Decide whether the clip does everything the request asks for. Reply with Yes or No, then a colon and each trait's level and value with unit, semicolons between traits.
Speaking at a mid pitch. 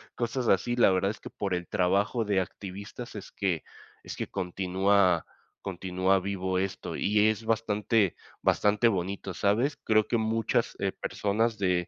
No: low, 100 Hz